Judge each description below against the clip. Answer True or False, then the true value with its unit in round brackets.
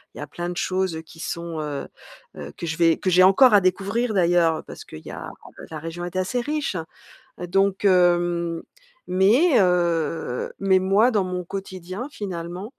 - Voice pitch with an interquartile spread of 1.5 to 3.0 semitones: True (2.6 semitones)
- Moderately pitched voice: True (180 Hz)